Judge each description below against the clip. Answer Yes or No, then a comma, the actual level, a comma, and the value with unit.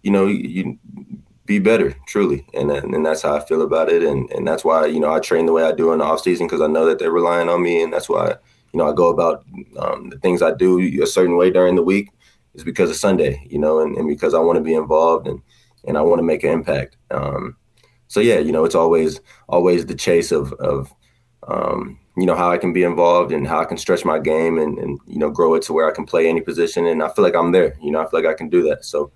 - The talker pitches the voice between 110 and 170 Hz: No, very low, 90 Hz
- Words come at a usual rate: No, fast, 280 wpm